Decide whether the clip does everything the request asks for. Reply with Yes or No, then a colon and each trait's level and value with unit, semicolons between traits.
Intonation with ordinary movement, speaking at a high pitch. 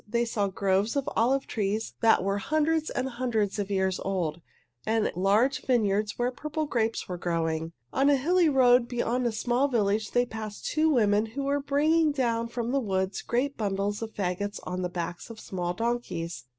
Yes: average, 4.7 semitones; high, 225 Hz